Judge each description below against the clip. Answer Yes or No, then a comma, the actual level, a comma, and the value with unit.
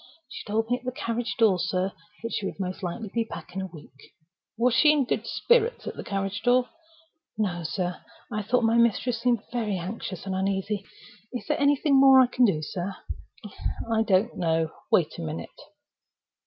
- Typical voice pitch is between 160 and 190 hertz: No, high, 215 Hz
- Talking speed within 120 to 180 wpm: No, average, 190 wpm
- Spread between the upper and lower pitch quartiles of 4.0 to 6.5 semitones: Yes, average, 4.7 semitones